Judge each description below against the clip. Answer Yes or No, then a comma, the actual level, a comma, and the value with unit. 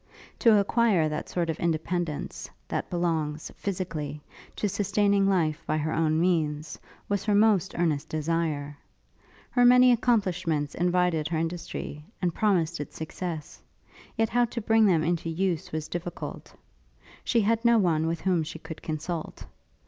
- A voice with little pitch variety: No, average, 4.1 semitones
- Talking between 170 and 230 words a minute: No, average, 150 wpm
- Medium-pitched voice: Yes, medium, 170 Hz